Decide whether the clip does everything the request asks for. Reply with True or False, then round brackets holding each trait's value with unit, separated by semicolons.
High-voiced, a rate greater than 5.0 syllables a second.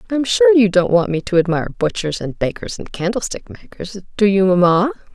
True (195 Hz; 5.6 syllables/s)